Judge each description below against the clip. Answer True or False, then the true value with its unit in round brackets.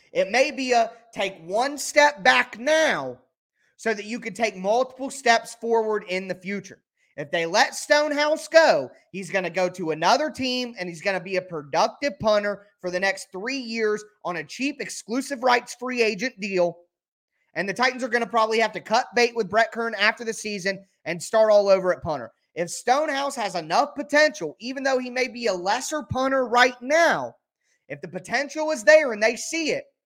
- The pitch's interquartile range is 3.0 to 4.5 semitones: False (5.4 semitones)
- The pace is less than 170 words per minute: False (200 wpm)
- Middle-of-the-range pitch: False (225 Hz)